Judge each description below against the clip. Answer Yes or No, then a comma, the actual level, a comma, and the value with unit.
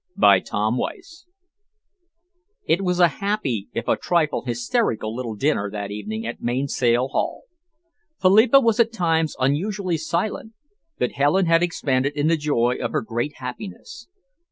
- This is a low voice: No, medium, 145 Hz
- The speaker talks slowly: No, average, 145 wpm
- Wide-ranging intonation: Yes, wide, 7.3 semitones